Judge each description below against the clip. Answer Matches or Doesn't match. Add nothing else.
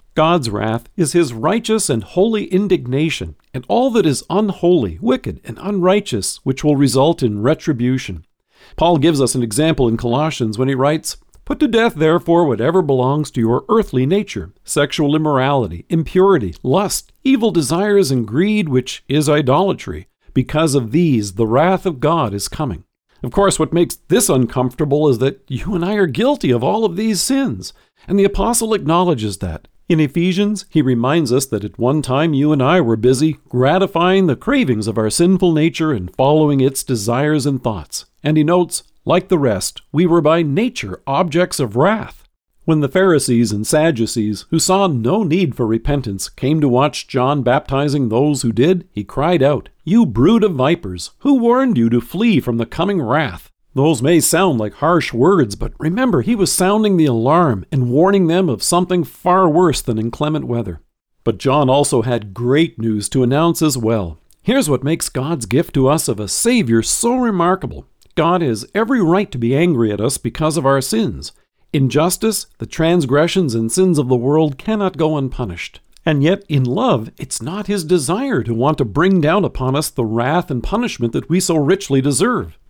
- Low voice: Doesn't match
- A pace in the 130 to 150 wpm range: Doesn't match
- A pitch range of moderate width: Doesn't match